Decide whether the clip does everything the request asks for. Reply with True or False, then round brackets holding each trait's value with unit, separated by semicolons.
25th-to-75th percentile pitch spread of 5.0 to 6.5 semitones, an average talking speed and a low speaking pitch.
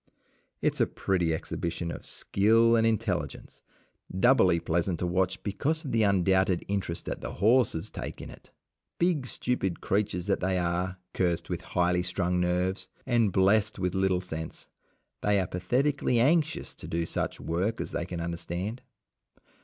False (4.1 semitones; 160 wpm; 95 Hz)